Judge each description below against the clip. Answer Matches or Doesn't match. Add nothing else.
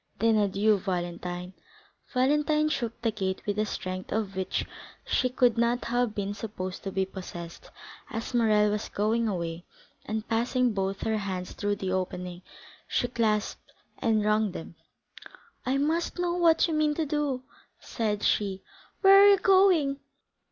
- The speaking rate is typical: Matches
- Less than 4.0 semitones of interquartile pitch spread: Doesn't match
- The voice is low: Doesn't match